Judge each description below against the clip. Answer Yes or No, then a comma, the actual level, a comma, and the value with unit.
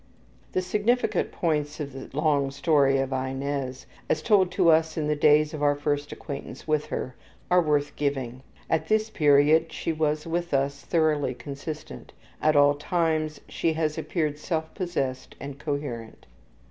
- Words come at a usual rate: Yes, average, 160 wpm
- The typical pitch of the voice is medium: Yes, medium, 150 Hz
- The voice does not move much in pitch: Yes, narrow, 2.2 semitones